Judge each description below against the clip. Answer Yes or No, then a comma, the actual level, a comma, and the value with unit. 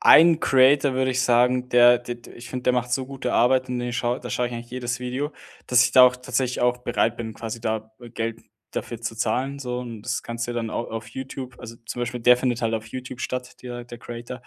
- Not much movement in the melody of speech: Yes, narrow, 1.3 semitones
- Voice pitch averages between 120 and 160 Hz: Yes, low, 125 Hz